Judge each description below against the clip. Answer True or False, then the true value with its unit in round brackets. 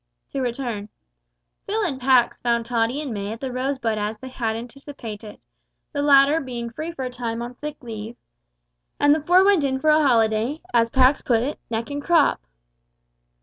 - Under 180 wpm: False (185 wpm)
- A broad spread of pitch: False (3.8 semitones)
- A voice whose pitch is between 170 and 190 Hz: False (255 Hz)